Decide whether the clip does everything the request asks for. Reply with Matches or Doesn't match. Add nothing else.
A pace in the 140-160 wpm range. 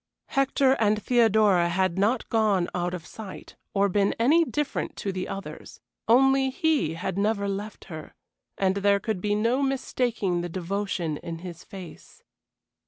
Matches